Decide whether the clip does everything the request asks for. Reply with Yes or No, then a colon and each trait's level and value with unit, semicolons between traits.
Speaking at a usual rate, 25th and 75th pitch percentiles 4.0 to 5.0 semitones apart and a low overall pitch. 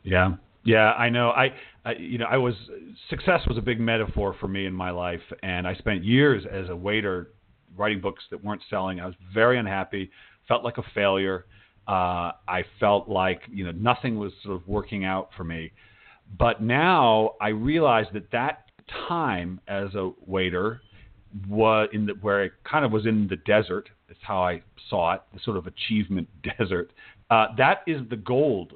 No: average, 190 wpm; average, 3.1 semitones; low, 100 Hz